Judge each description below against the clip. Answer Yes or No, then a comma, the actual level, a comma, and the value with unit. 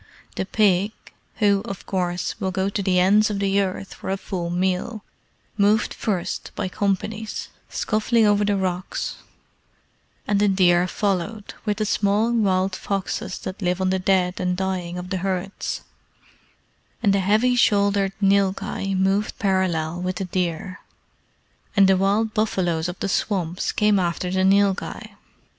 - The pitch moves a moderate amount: No, narrow, 1.9 semitones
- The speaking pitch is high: Yes, high, 195 Hz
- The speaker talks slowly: No, average, 150 wpm